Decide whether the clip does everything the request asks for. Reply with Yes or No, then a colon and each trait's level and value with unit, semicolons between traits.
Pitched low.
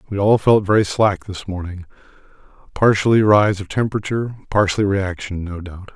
Yes: low, 100 Hz